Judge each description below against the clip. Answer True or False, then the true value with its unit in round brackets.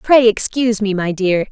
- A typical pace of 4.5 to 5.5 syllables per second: True (5.0 syllables/s)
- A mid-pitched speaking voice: False (210 Hz)